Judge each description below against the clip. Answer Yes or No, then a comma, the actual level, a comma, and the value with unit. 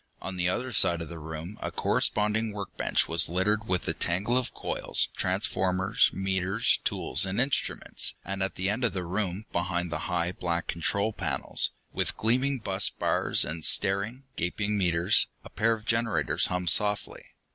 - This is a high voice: No, very low, 95 Hz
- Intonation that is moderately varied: Yes, average, 3.3 semitones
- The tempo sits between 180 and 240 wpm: No, average, 165 wpm